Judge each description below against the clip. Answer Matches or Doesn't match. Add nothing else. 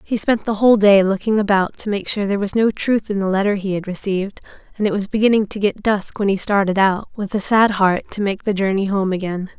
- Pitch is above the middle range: Matches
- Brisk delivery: Matches